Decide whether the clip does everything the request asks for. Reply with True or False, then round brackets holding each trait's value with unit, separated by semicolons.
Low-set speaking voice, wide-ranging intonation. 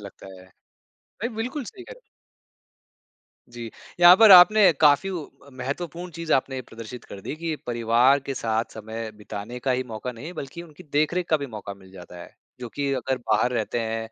True (130 Hz; 6.9 semitones)